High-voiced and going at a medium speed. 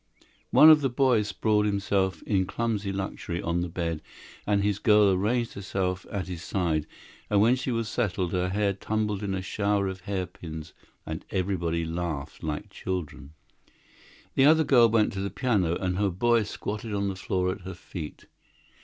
No: low, 100 Hz; average, 175 wpm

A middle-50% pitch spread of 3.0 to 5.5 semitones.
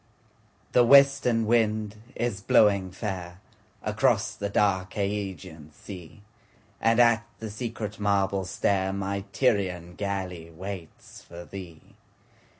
No: narrow, 2.6 semitones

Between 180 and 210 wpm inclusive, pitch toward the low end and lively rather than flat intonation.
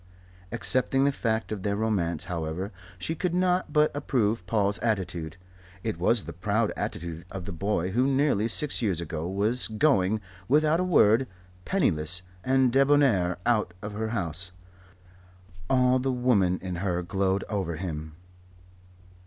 No: average, 145 wpm; low, 105 Hz; wide, 6.1 semitones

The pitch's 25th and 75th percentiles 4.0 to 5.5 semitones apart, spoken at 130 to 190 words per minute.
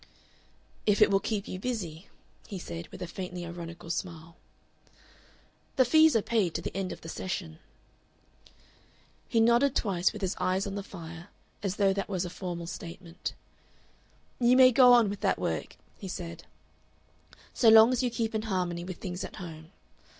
Yes: average, 4.3 semitones; average, 175 wpm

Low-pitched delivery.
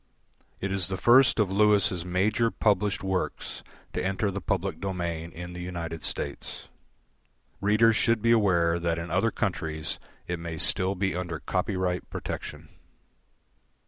Yes: very low, 95 Hz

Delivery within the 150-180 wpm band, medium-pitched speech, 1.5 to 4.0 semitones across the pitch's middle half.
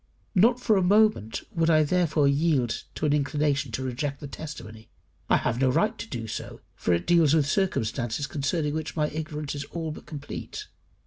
No: average, 190 wpm; medium, 150 Hz; average, 3.5 semitones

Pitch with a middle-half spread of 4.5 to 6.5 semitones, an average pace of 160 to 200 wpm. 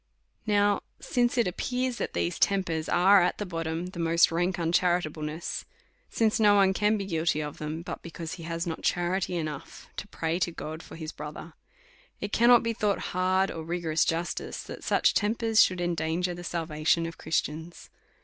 No: average, 3.4 semitones; average, 180 wpm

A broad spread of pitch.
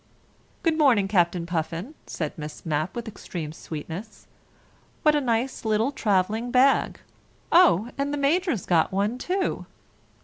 Yes: wide, 8.2 semitones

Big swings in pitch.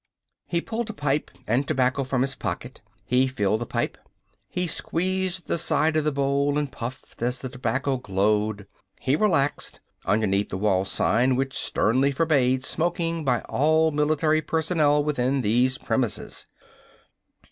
No: average, 4.0 semitones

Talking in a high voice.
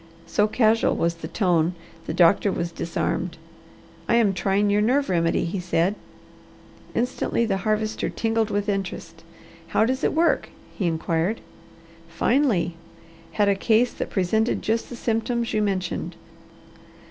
Yes: high, 205 Hz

